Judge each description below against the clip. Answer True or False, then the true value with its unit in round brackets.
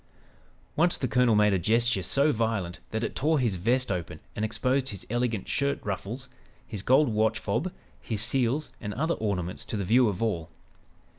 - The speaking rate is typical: True (180 wpm)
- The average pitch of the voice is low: True (115 Hz)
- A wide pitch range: False (4.1 semitones)